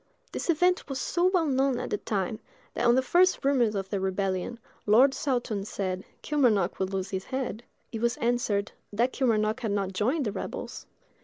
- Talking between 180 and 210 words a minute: Yes, average, 185 wpm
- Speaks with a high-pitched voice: Yes, high, 230 Hz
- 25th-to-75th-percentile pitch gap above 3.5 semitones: Yes, average, 5.0 semitones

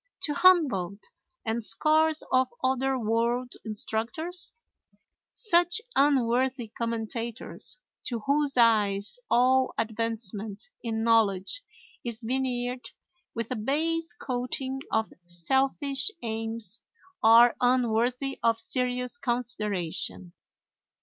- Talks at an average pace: No, slow, 90 wpm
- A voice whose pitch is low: No, high, 240 Hz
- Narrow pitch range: No, average, 3.1 semitones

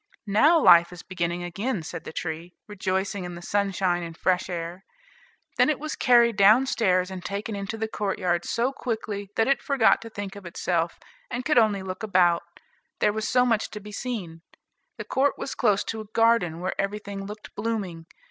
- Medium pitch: No, high, 200 Hz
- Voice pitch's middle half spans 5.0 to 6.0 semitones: No, average, 3.9 semitones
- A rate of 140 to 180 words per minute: No, average, 190 wpm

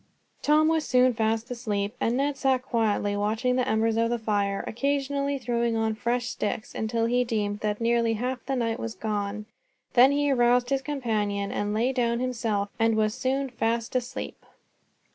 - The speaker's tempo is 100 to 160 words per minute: No, average, 175 wpm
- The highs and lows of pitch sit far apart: No, average, 2.7 semitones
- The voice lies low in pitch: No, high, 235 Hz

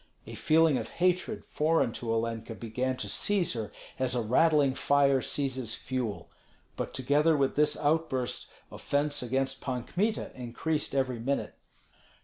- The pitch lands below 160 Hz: Yes, low, 135 Hz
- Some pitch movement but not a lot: Yes, average, 3.6 semitones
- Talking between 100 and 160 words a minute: Yes, average, 140 wpm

